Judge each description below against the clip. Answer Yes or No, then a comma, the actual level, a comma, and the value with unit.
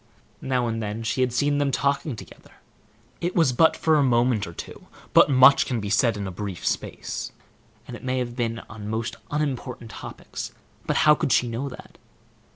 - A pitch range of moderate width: Yes, average, 3.5 semitones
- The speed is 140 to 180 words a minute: No, average, 190 wpm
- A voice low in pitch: Yes, low, 125 Hz